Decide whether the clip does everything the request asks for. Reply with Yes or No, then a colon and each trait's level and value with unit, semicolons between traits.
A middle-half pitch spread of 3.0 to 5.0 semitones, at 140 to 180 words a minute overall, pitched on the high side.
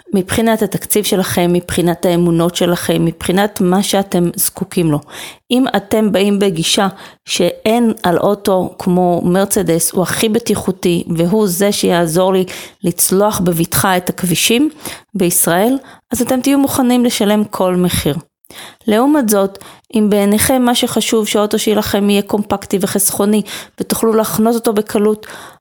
No: average, 3.4 semitones; average, 125 wpm; high, 200 Hz